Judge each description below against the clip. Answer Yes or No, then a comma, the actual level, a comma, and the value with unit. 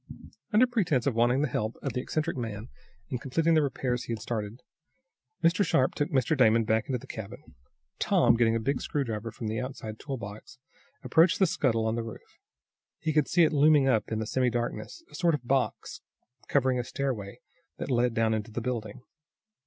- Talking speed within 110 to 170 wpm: No, average, 190 wpm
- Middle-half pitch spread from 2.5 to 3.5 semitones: No, average, 4.0 semitones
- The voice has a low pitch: Yes, low, 125 Hz